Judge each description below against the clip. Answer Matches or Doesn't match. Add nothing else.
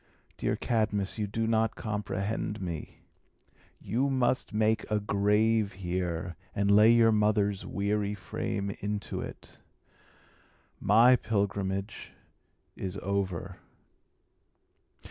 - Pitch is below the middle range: Matches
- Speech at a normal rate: Doesn't match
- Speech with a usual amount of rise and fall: Doesn't match